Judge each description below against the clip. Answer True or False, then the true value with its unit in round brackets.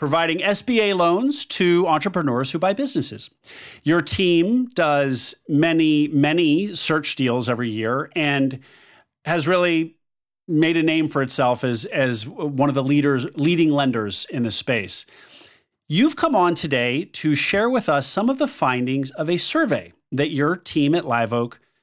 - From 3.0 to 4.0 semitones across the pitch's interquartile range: False (4.7 semitones)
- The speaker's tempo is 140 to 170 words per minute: True (155 wpm)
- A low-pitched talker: False (155 Hz)